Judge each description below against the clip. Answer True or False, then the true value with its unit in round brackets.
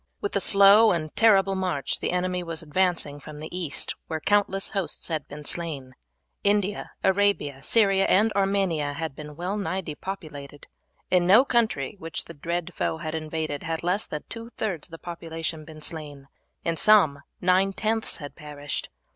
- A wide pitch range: False (4.3 semitones)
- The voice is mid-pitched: True (170 Hz)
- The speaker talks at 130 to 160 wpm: False (170 wpm)